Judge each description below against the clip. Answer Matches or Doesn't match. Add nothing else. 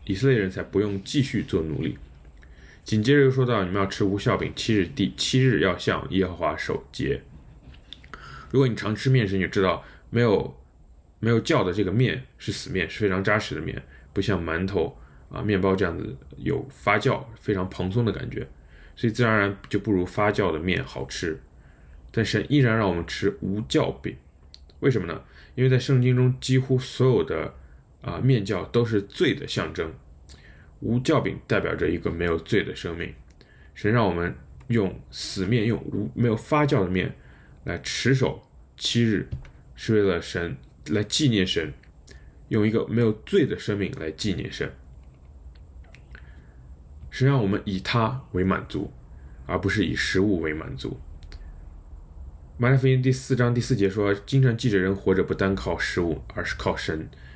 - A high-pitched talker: Doesn't match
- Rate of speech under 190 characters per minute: Doesn't match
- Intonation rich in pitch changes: Matches